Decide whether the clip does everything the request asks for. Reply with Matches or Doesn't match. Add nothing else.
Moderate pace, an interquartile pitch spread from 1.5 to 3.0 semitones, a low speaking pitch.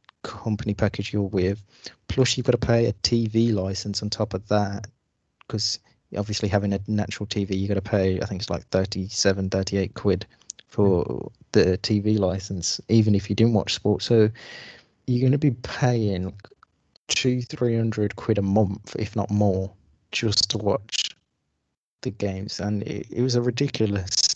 Matches